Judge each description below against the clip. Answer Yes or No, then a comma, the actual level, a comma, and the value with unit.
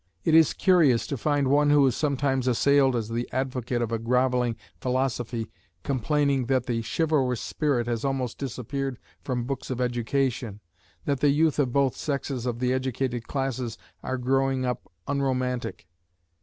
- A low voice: Yes, low, 130 Hz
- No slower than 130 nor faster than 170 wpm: Yes, average, 155 wpm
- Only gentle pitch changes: Yes, narrow, 2.3 semitones